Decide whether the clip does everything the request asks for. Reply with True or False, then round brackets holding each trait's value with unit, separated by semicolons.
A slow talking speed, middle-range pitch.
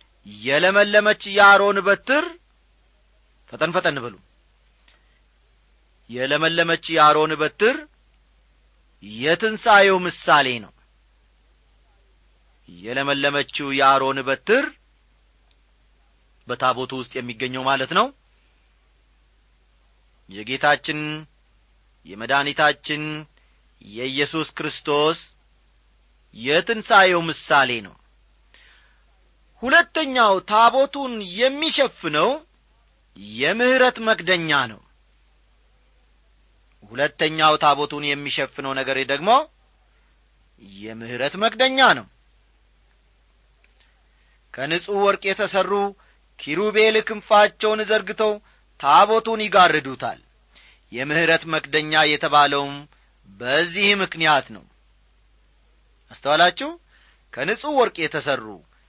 True (60 wpm; 150 Hz)